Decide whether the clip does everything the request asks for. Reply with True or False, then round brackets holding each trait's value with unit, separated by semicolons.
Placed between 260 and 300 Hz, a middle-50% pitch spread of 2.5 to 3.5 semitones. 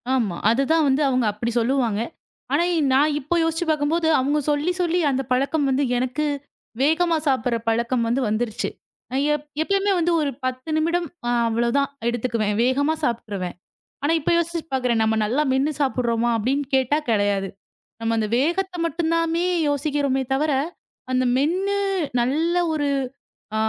False (270 Hz; 4.8 semitones)